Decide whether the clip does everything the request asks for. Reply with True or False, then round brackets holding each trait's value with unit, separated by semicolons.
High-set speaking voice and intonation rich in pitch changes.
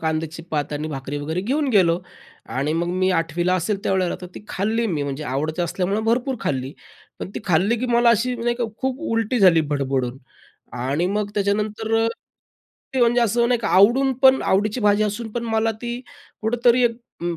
True (205 Hz; 6.3 semitones)